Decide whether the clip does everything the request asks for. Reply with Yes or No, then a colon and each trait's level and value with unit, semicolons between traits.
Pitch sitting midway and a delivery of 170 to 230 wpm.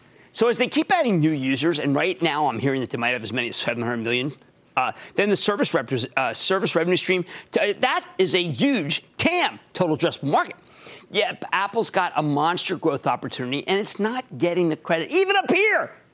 Yes: medium, 175 Hz; fast, 205 wpm